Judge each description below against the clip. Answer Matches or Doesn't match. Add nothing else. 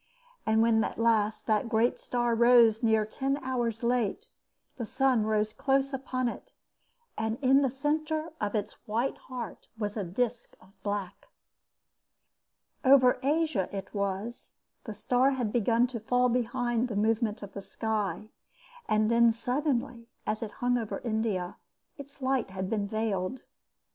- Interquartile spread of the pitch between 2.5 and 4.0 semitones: Matches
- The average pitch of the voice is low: Doesn't match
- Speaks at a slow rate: Doesn't match